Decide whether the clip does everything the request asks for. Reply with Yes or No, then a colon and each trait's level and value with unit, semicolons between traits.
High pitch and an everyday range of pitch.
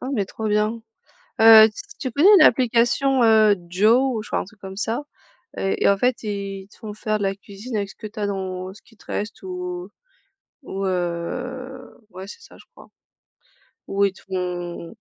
Yes: high, 210 Hz; average, 3.1 semitones